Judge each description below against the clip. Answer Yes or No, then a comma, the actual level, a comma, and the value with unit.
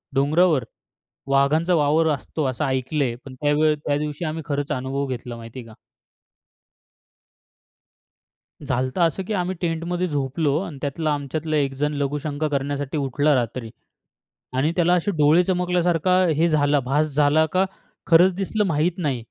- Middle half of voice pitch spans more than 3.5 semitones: No, average, 3.2 semitones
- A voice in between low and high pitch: Yes, medium, 150 Hz